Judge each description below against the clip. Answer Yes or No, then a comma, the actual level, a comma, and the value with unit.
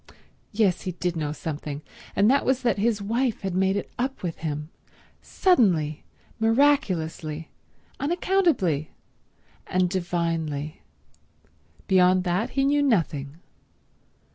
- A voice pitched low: No, medium, 185 Hz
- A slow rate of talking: Yes, slow, 110 wpm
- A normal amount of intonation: No, wide, 6.7 semitones